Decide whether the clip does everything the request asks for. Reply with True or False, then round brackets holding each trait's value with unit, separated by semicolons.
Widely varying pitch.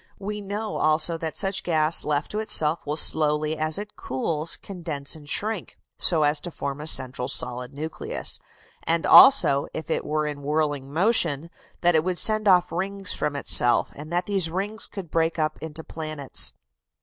False (3.7 semitones)